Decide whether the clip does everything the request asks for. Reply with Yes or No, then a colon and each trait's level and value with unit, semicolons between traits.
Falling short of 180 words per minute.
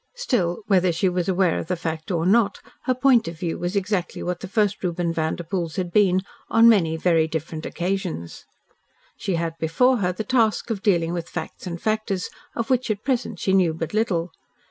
No: average, 195 wpm